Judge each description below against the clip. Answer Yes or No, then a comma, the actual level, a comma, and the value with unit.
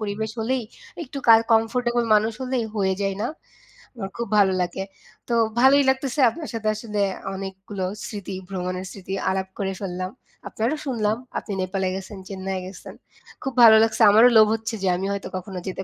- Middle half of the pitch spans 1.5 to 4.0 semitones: Yes, average, 3.3 semitones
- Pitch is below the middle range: No, high, 210 Hz